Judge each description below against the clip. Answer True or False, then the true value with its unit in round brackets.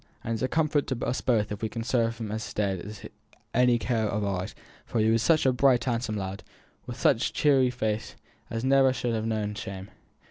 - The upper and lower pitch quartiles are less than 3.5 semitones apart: True (2.9 semitones)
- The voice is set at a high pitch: False (115 Hz)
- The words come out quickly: True (225 wpm)